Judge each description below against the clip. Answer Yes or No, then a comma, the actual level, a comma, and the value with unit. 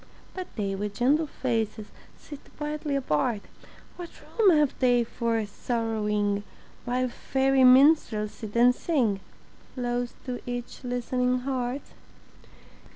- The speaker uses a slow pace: Yes, slow, 115 wpm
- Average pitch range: Yes, average, 3.3 semitones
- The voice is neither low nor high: No, high, 245 Hz